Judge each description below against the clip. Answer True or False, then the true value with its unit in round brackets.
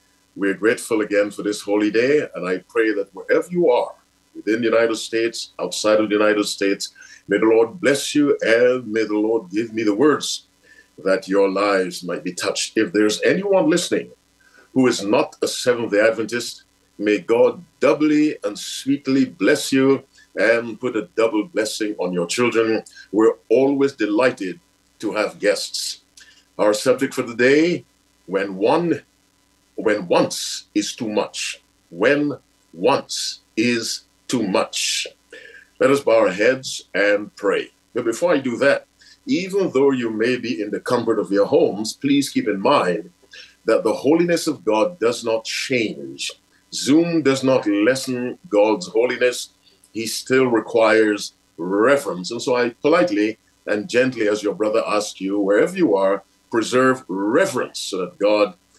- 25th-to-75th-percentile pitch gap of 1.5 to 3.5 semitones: False (5.3 semitones)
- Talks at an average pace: True (160 wpm)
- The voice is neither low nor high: False (115 Hz)